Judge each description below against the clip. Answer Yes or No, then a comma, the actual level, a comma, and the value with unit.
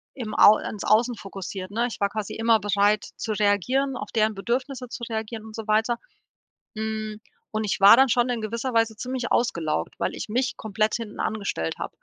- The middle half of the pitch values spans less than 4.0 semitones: Yes, narrow, 2.4 semitones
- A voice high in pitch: Yes, high, 220 Hz